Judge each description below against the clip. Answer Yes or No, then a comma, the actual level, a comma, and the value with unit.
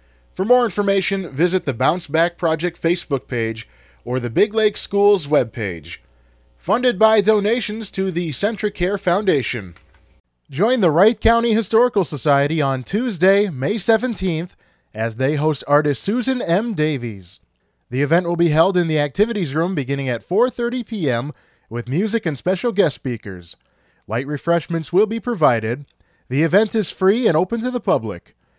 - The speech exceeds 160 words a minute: No, average, 155 wpm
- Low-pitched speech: No, medium, 165 Hz